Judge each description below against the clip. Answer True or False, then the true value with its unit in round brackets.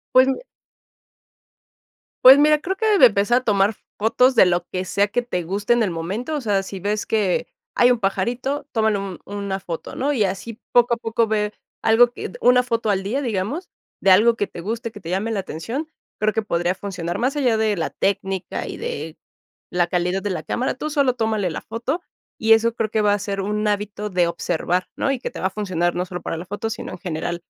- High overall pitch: True (210 Hz)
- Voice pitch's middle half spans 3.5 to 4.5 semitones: True (4.1 semitones)